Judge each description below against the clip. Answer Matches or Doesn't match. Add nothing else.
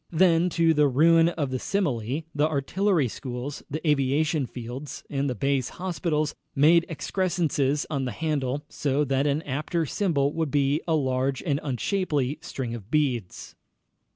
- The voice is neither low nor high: Matches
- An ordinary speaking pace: Matches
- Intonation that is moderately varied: Matches